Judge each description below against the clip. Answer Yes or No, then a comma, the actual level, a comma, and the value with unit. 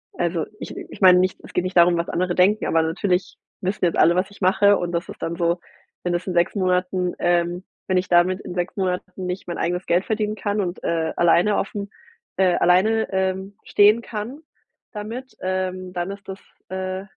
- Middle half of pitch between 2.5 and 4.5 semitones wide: No, narrow, 2.0 semitones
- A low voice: No, medium, 185 Hz